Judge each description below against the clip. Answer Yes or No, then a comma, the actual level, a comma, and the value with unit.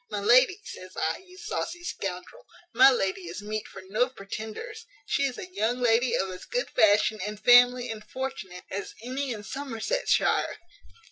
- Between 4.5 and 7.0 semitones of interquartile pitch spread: Yes, average, 5.0 semitones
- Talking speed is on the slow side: No, average, 165 wpm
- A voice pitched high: Yes, high, 240 Hz